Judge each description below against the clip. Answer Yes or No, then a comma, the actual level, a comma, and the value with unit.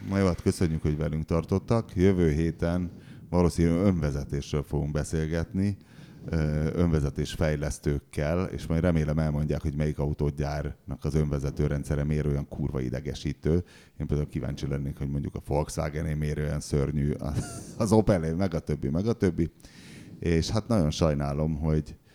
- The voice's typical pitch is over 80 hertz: No, very low, 75 Hz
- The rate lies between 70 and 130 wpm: No, average, 145 wpm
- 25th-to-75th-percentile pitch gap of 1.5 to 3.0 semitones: Yes, average, 2.7 semitones